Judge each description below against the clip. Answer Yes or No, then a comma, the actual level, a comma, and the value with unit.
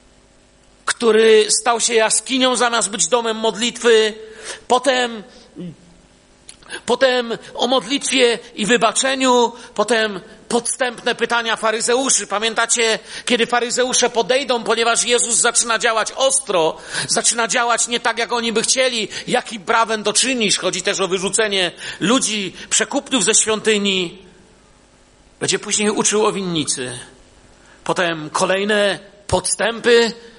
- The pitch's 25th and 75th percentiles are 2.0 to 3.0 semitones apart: Yes, narrow, 2.4 semitones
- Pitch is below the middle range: No, high, 230 Hz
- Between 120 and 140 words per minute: No, slow, 110 wpm